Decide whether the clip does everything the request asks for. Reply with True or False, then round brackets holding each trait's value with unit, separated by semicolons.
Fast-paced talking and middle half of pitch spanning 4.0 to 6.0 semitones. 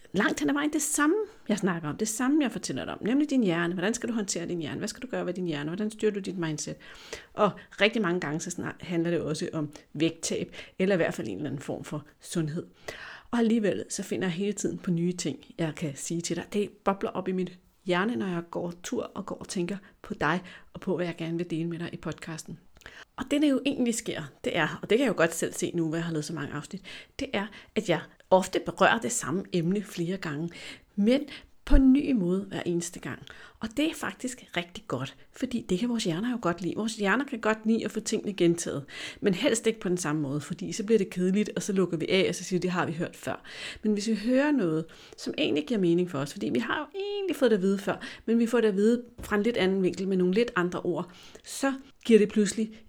True (260 wpm; 4.8 semitones)